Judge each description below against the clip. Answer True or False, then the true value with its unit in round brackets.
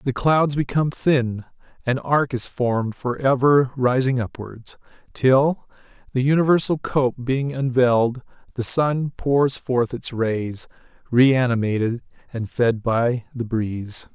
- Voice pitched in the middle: False (125 Hz)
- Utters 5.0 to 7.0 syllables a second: False (4.0 syllables/s)